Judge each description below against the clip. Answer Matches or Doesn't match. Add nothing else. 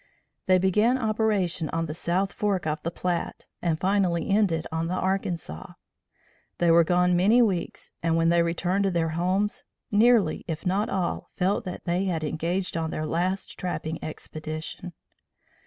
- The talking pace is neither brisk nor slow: Matches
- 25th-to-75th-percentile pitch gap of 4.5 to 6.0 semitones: Doesn't match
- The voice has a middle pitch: Matches